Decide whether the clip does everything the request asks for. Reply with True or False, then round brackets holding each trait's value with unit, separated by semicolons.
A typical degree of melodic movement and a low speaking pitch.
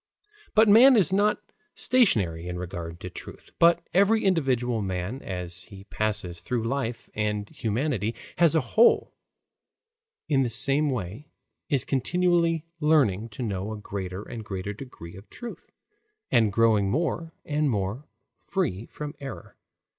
False (7.7 semitones; 120 Hz)